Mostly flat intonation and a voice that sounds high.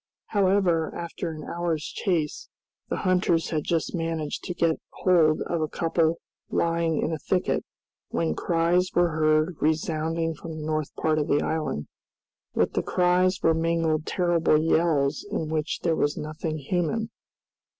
No: narrow, 1.9 semitones; medium, 165 Hz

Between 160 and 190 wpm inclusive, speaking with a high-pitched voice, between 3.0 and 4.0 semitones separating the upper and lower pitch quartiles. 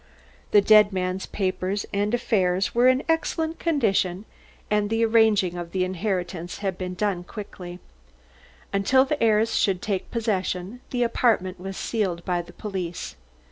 No: average, 145 wpm; high, 200 Hz; average, 3.6 semitones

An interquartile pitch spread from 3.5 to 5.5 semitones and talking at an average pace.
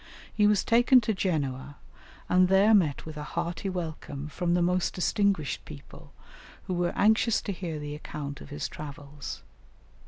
Yes: average, 4.9 semitones; average, 160 wpm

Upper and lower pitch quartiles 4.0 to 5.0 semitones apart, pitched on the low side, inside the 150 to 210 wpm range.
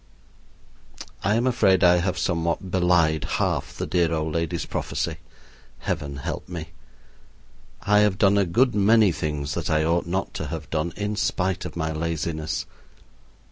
No: average, 3.6 semitones; very low, 85 Hz; average, 155 wpm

